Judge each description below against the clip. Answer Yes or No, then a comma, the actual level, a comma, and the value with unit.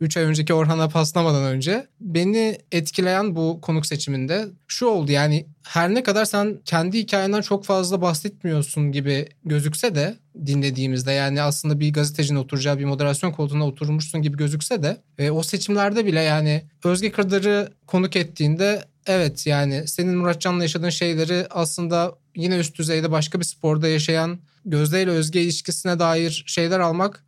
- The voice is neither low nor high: Yes, medium, 165 Hz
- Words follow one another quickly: Yes, fast, 150 wpm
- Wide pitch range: No, average, 3.5 semitones